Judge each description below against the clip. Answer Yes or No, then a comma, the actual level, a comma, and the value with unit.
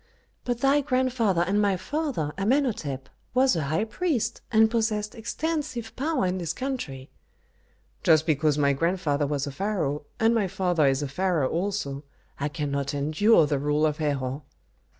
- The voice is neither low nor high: Yes, medium, 180 Hz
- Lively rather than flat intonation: Yes, wide, 7.8 semitones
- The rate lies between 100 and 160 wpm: Yes, average, 155 wpm